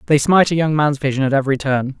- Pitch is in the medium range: Yes, medium, 145 Hz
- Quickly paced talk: Yes, fast, 270 wpm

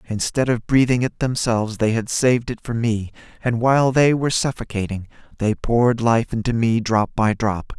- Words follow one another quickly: No, average, 185 wpm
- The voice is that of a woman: No, male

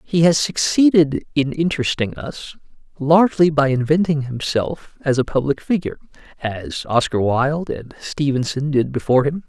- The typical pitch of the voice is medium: Yes, medium, 145 Hz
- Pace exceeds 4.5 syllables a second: Yes, 5.0 syllables/s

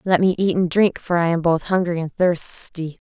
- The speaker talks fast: Yes, fast, 235 wpm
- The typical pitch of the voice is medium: Yes, medium, 175 Hz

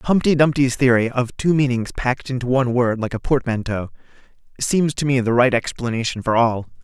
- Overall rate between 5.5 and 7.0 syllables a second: Yes, 5.6 syllables/s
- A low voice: Yes, low, 125 Hz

